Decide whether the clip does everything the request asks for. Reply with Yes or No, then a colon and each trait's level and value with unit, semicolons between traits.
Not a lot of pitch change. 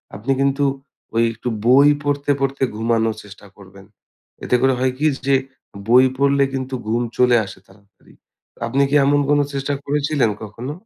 No: average, 3.7 semitones